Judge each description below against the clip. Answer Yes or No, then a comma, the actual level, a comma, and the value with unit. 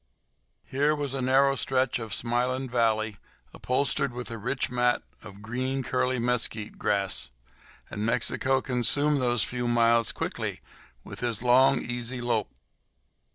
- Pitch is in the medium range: No, low, 125 Hz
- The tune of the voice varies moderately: No, narrow, 2.2 semitones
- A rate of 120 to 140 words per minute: Yes, slow, 135 wpm